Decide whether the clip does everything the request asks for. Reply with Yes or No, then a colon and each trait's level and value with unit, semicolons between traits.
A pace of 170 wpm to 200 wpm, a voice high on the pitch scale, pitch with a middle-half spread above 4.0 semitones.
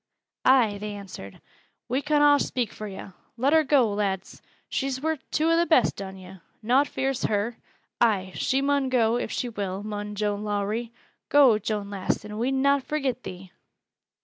Yes: average, 175 wpm; high, 230 Hz; average, 4.8 semitones